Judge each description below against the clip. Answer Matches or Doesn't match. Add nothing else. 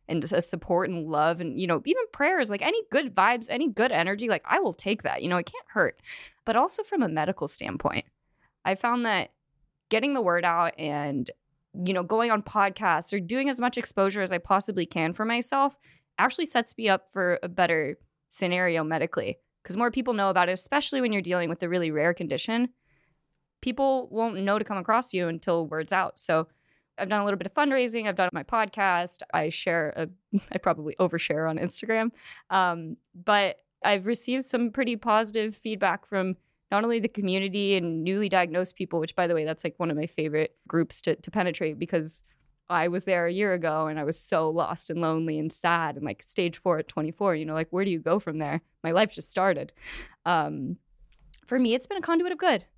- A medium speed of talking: Doesn't match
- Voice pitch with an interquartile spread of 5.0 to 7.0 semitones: Matches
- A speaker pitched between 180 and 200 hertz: Matches